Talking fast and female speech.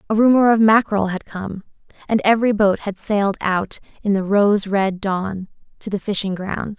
No: average, 185 wpm; female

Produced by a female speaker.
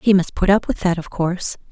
Yes: female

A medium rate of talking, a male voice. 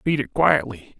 Yes: average, 180 wpm; male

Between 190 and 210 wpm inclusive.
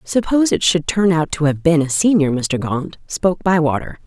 Yes: fast, 205 wpm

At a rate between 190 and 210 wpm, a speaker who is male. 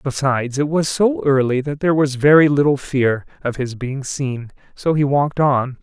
Yes: average, 195 wpm; male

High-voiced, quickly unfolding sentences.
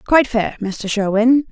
No: high, 230 Hz; average, 160 wpm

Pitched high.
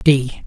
No: low, 135 Hz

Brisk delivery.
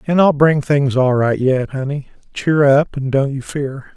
No: average, 195 wpm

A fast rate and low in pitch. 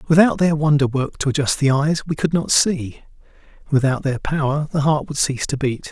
No: fast, 215 wpm; medium, 145 Hz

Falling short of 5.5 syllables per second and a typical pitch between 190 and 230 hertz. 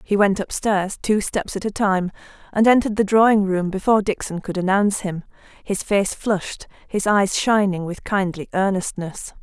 Yes: 5.0 syllables/s; high, 195 Hz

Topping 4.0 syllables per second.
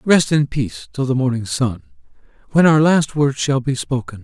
Yes: 5.0 syllables/s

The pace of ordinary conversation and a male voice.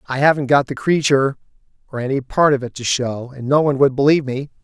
No: fast, 235 wpm; male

